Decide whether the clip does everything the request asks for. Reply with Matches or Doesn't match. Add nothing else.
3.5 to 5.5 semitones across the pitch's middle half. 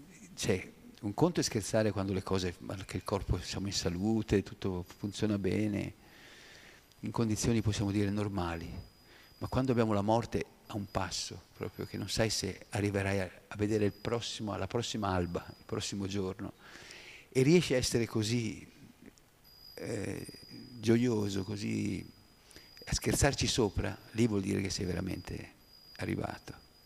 Doesn't match